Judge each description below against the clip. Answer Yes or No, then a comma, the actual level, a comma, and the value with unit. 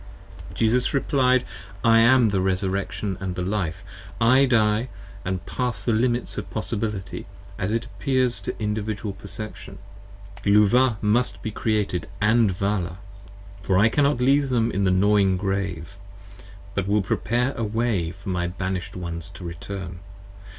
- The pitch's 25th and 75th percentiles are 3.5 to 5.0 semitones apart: Yes, average, 3.8 semitones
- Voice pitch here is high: No, low, 105 Hz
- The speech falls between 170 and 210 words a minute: No, average, 145 wpm